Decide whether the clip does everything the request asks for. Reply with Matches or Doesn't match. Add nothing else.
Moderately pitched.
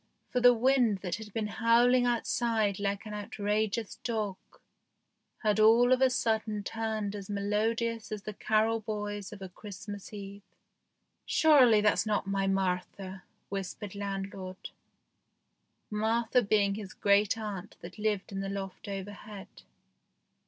Doesn't match